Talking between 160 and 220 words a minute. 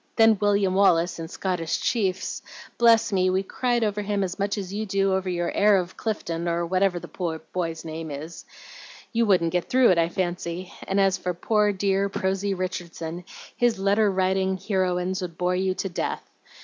Yes: average, 185 wpm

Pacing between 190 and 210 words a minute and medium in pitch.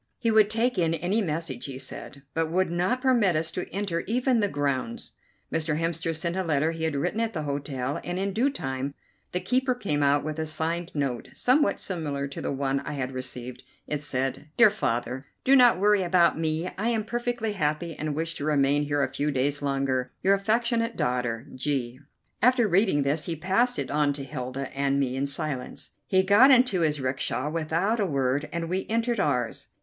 Yes: average, 200 wpm; medium, 160 Hz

